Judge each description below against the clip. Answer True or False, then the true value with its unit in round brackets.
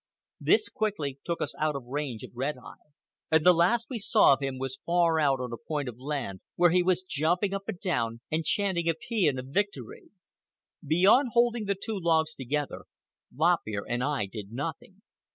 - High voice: False (160 Hz)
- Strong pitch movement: True (5.7 semitones)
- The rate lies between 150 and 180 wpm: False (195 wpm)